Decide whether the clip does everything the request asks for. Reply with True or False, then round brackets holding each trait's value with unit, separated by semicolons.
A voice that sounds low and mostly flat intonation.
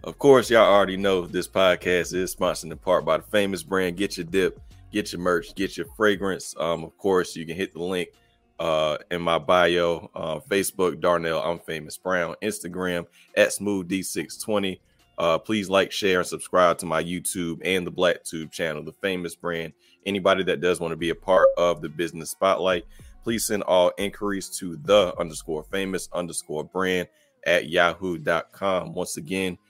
True (90 Hz; 2.3 semitones)